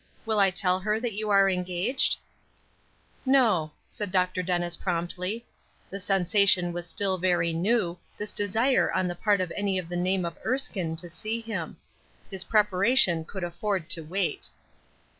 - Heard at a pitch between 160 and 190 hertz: Yes, medium, 185 Hz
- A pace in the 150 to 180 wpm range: Yes, average, 160 wpm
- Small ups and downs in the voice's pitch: No, average, 3.0 semitones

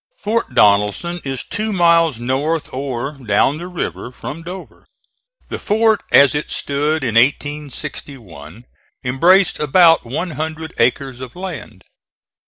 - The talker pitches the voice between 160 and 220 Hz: No, medium, 145 Hz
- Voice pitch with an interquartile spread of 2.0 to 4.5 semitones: No, average, 5.1 semitones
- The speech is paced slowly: Yes, slow, 125 wpm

